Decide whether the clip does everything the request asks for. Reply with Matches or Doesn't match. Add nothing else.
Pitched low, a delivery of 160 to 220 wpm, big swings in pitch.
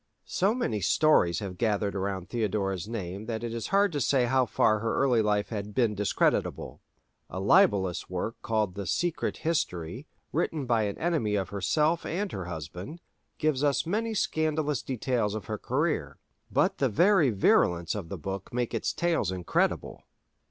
Matches